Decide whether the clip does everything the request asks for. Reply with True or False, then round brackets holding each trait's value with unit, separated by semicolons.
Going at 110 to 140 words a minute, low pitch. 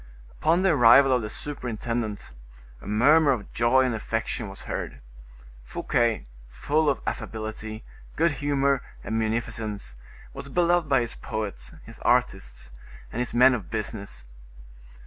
True (135 wpm; 115 Hz)